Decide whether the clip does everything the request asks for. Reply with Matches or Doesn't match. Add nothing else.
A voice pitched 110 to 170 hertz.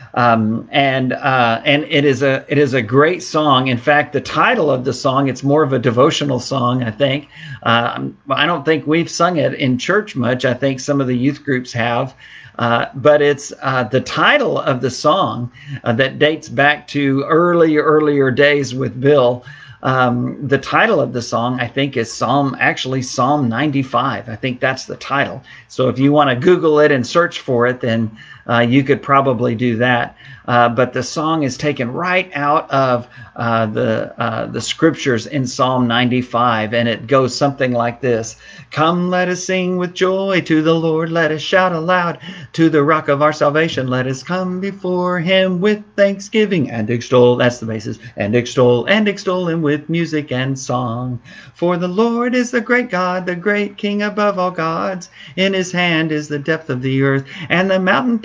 Matches